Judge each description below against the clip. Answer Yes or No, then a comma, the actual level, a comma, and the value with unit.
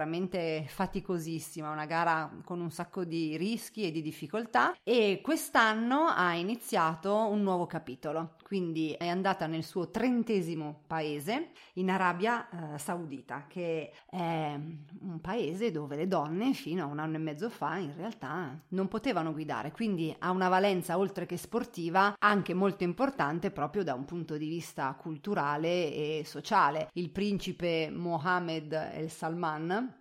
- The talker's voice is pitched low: No, medium, 175 Hz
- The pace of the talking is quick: No, average, 145 wpm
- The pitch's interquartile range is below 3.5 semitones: No, average, 3.8 semitones